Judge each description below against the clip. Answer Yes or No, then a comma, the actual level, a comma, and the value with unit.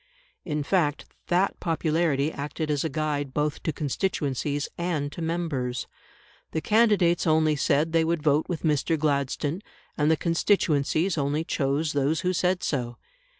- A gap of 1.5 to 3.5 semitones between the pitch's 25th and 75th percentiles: Yes, average, 2.7 semitones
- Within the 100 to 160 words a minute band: Yes, average, 150 wpm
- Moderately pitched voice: Yes, medium, 155 Hz